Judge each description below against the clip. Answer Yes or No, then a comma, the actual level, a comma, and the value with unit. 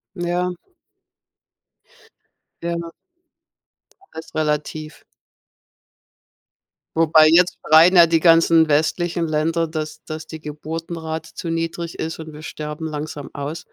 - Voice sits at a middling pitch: Yes, medium, 160 Hz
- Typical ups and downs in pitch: No, narrow, 1.3 semitones